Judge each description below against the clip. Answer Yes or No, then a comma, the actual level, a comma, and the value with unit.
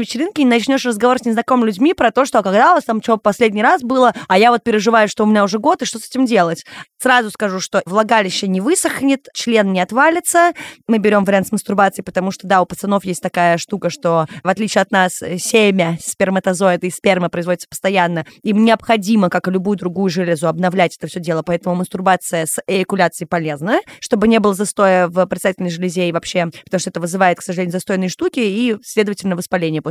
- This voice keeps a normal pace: No, fast, 205 wpm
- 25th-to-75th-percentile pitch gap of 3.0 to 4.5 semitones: Yes, average, 4.1 semitones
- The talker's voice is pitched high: Yes, high, 195 Hz